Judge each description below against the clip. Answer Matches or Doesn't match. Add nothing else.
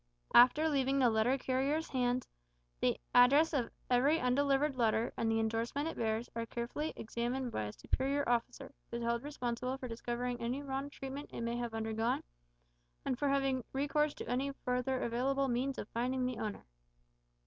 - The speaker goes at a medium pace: Matches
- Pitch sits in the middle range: Doesn't match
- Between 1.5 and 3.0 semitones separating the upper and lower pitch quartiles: Matches